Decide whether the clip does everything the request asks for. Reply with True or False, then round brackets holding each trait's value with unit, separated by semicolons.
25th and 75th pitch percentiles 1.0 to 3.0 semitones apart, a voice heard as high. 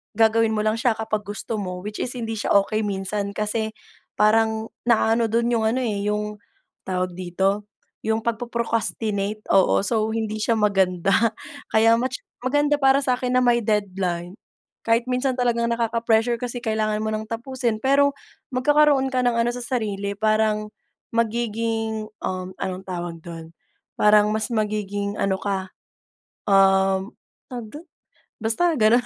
True (2.5 semitones; 220 Hz)